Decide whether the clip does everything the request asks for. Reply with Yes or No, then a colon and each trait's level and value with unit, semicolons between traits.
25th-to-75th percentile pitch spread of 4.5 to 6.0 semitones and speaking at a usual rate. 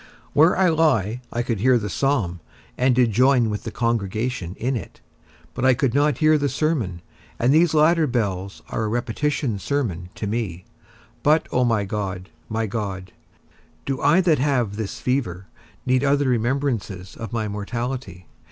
Yes: average, 5.2 semitones; average, 165 wpm